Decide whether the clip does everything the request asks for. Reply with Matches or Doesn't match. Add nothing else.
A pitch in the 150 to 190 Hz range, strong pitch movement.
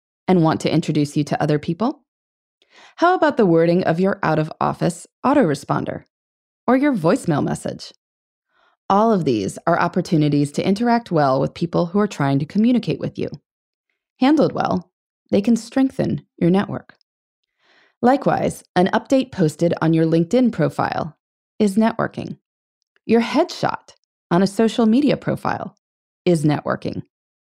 Matches